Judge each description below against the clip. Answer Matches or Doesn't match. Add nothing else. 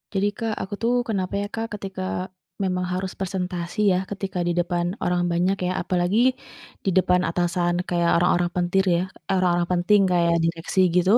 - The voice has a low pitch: Doesn't match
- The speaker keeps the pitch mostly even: Matches